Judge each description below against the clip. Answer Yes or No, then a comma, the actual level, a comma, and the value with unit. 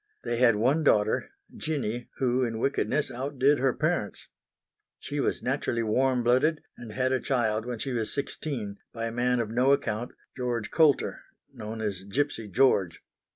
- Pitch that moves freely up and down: No, average, 3.3 semitones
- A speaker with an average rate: Yes, average, 160 wpm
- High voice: No, low, 120 Hz